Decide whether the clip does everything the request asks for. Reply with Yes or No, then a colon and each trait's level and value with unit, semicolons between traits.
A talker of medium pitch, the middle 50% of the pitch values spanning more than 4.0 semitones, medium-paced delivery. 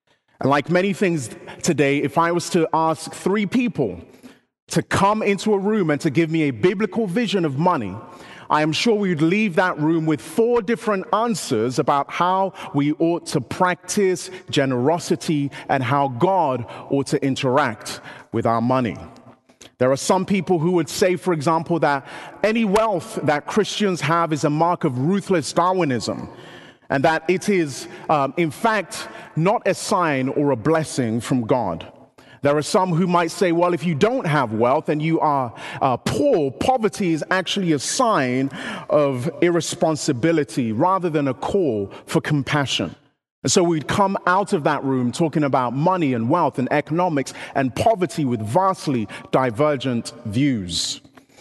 Yes: medium, 165 Hz; average, 4.7 semitones; average, 165 wpm